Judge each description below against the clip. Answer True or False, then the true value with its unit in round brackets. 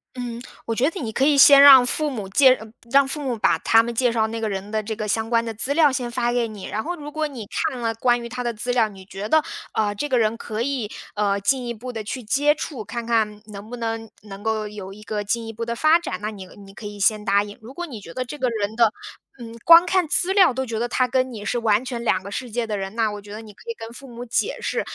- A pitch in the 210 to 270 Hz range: True (230 Hz)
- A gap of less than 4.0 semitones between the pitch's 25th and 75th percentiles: True (3.4 semitones)